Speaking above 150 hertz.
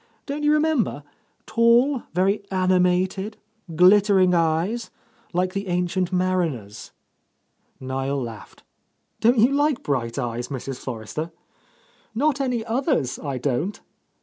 Yes: medium, 185 Hz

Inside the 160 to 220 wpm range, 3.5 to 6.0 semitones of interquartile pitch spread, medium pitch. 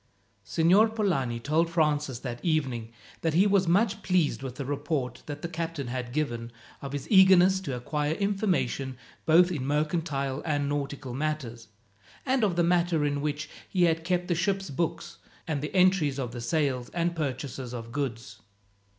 Yes: average, 170 wpm; average, 4.6 semitones; medium, 150 Hz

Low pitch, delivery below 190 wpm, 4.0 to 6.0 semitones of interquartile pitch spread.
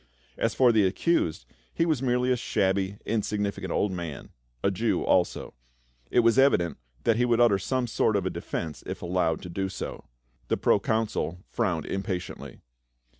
Yes: low, 100 Hz; average, 170 wpm; average, 4.6 semitones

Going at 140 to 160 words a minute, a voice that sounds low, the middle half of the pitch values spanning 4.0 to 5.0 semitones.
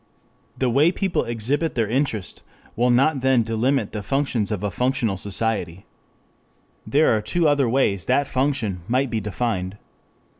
Yes: average, 150 wpm; low, 120 Hz; average, 4.5 semitones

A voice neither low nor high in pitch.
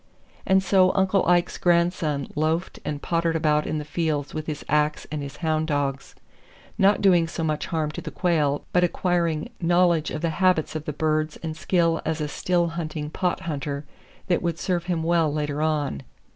Yes: medium, 160 Hz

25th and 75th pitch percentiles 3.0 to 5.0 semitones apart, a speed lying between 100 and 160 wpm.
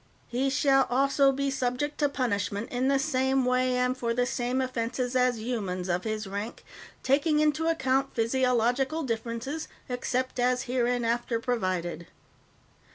No: narrow, 2.6 semitones; average, 140 wpm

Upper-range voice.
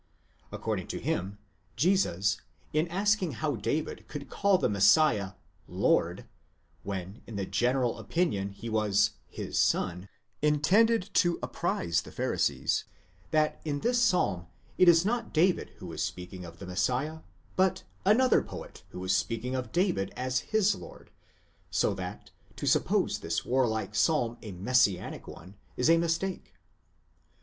No: low, 125 Hz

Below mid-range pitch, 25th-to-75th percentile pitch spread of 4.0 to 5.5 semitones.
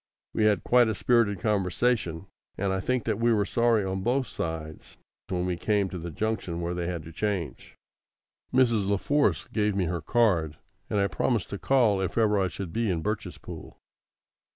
Yes: low, 100 Hz; average, 4.3 semitones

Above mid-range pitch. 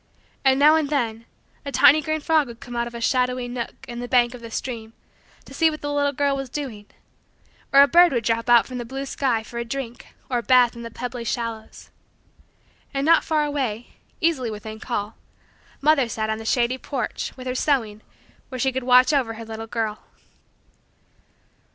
Yes: very high, 250 Hz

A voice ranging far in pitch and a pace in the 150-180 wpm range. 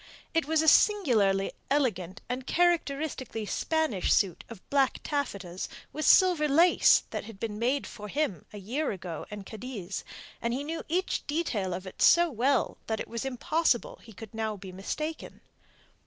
Yes: wide, 7.1 semitones; average, 165 wpm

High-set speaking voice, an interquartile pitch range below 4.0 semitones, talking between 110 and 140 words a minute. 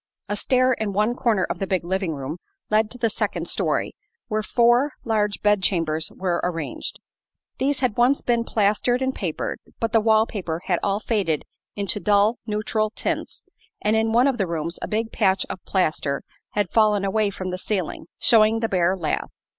No: high, 210 Hz; average, 3.4 semitones; average, 185 wpm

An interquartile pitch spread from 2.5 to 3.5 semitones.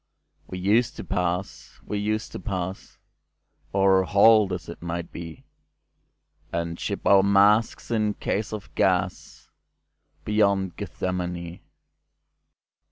Yes: average, 2.9 semitones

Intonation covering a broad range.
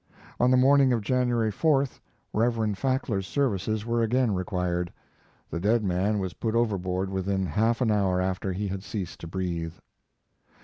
No: average, 4.2 semitones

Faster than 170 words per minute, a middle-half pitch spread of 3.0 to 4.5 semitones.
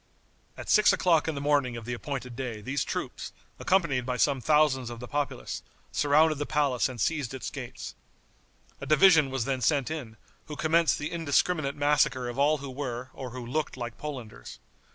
Yes: average, 185 wpm; average, 3.3 semitones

